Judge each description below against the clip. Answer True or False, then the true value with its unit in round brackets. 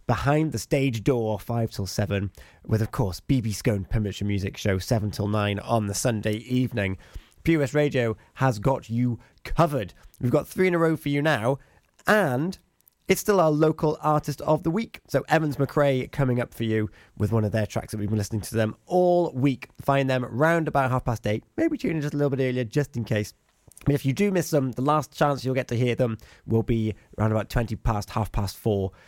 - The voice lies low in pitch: True (125 Hz)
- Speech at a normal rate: False (225 wpm)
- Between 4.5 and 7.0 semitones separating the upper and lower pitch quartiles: True (5.2 semitones)